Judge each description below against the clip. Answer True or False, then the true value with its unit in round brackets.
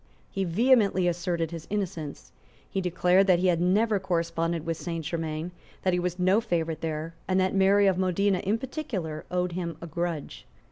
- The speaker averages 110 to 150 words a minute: False (180 wpm)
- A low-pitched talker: False (180 Hz)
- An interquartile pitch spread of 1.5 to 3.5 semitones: True (2.5 semitones)